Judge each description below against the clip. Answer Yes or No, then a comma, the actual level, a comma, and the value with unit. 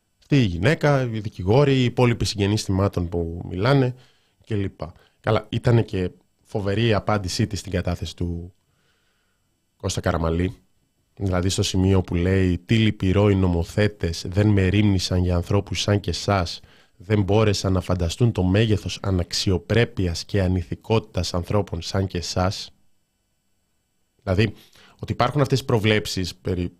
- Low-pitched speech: Yes, low, 100 Hz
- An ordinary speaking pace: Yes, average, 135 wpm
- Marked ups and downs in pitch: No, average, 3.0 semitones